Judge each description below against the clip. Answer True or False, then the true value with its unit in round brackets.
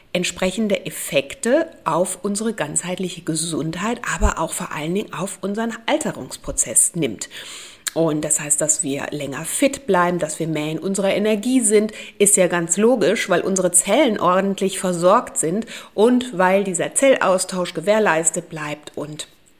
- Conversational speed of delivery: True (145 wpm)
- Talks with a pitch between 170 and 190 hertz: True (185 Hz)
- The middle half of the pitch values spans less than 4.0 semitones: False (4.5 semitones)